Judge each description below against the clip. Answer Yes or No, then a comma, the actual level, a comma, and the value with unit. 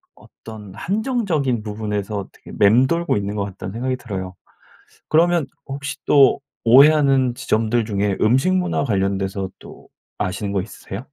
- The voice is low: Yes, low, 115 Hz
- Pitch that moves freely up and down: Yes, wide, 5.8 semitones